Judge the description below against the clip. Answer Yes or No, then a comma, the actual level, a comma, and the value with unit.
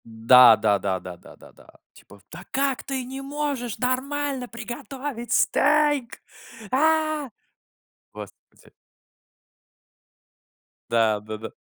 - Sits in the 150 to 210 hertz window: No, very high, 250 Hz